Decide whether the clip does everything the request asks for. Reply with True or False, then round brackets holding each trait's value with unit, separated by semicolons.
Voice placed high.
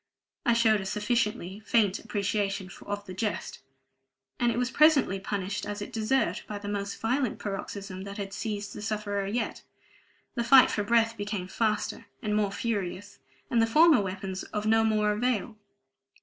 True (210 Hz)